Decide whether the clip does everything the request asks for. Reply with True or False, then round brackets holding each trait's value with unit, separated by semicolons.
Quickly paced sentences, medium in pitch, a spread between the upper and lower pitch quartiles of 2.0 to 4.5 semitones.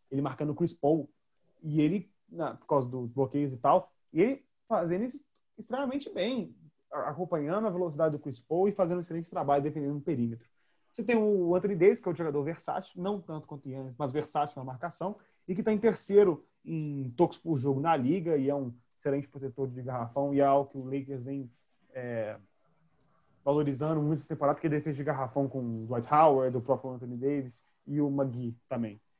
True (205 wpm; 150 Hz; 4.2 semitones)